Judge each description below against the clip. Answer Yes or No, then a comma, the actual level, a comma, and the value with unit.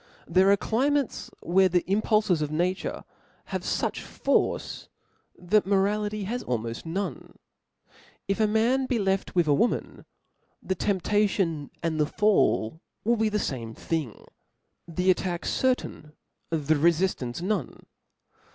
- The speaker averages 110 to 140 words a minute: Yes, slow, 135 wpm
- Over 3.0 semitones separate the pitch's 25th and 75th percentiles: Yes, average, 4.6 semitones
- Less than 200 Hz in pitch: Yes, high, 190 Hz